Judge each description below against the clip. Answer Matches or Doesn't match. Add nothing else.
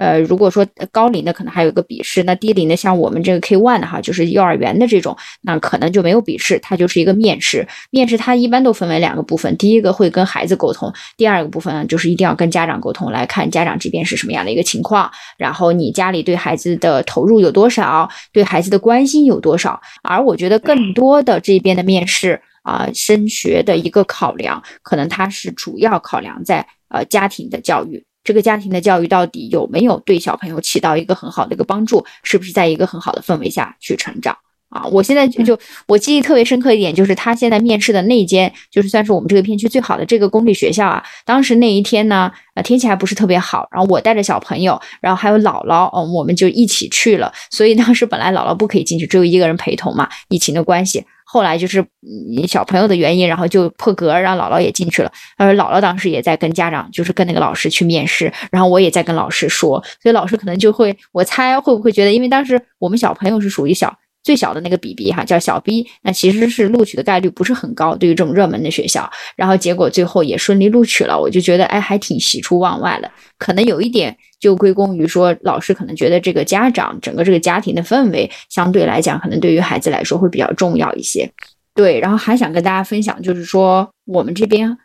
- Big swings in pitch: Doesn't match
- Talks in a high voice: Matches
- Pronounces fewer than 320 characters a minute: Doesn't match